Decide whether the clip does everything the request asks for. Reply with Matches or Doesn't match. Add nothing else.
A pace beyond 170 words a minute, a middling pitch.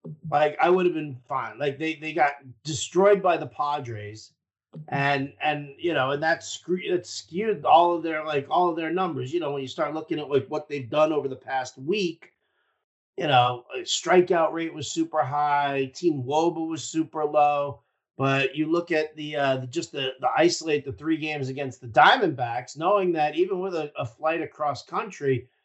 Matches